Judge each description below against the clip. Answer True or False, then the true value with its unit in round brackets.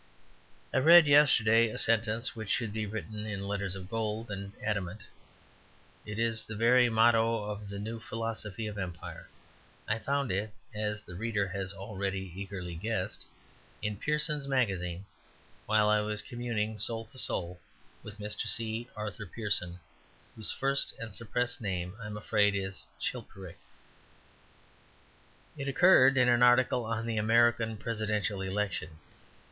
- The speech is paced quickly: False (145 wpm)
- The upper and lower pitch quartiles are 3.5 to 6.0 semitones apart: False (2.6 semitones)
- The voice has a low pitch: True (110 Hz)